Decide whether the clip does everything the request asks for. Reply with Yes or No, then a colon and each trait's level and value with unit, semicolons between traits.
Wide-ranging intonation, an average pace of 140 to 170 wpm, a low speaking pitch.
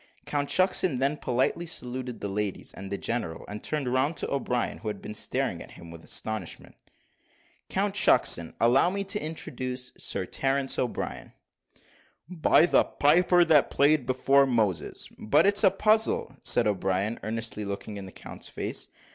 Yes: wide, 6.4 semitones; average, 160 wpm; low, 125 Hz